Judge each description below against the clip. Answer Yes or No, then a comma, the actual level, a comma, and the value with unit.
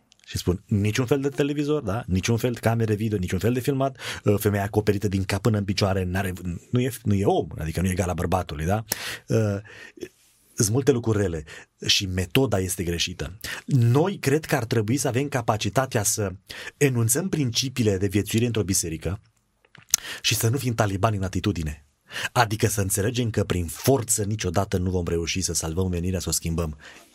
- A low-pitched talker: Yes, low, 105 Hz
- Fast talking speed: Yes, fast, 180 wpm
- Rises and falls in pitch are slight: No, average, 4.5 semitones